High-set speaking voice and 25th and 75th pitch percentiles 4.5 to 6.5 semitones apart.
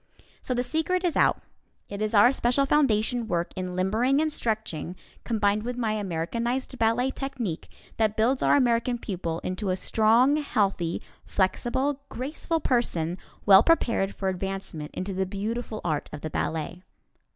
Yes: high, 220 Hz; average, 4.9 semitones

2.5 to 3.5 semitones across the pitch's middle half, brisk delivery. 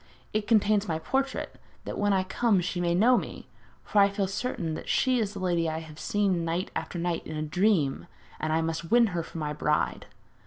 No: average, 4.1 semitones; fast, 220 wpm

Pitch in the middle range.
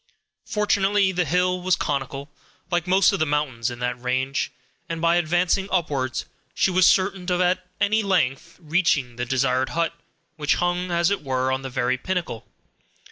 Yes: medium, 170 Hz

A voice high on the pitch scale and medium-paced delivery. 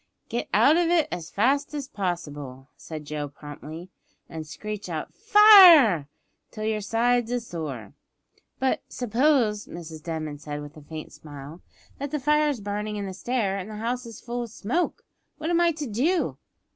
Yes: high, 215 Hz; average, 170 wpm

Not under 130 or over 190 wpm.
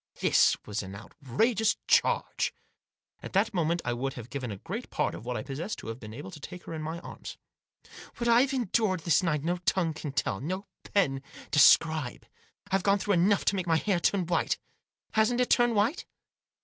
No: average, 200 wpm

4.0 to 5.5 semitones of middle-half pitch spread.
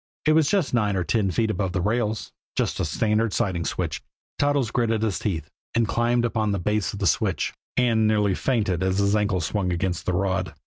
No: average, 3.4 semitones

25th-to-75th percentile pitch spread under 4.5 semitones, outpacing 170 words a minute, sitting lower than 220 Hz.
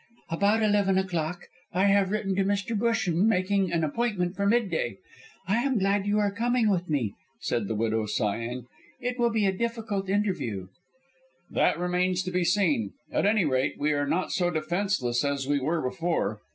No: average, 5.3 semitones; average, 180 wpm; medium, 185 Hz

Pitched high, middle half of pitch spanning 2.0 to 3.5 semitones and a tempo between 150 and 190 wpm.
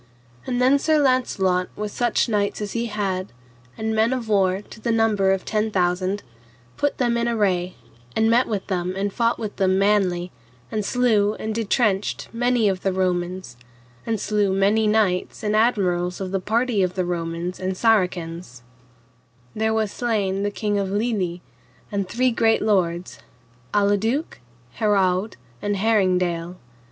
Yes: high, 205 Hz; average, 3.2 semitones; average, 155 wpm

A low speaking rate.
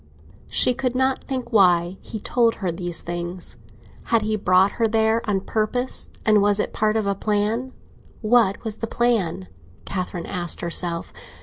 No: average, 165 wpm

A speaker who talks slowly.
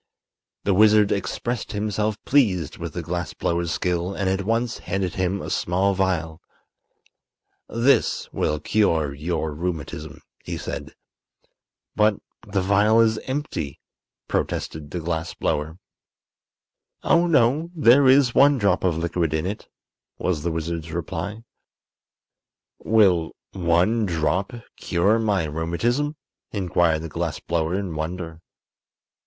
Yes: slow, 125 wpm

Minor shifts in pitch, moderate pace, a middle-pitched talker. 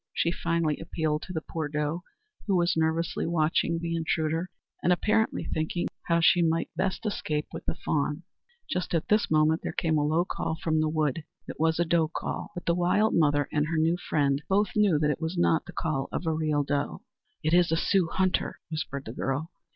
No: narrow, 2.1 semitones; fast, 210 wpm; medium, 160 Hz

